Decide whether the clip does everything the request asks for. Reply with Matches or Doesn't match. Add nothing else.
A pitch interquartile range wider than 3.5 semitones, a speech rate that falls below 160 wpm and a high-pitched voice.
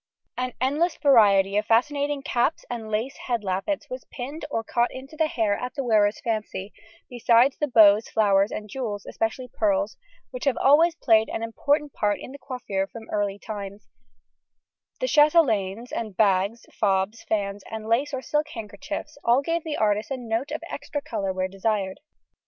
Doesn't match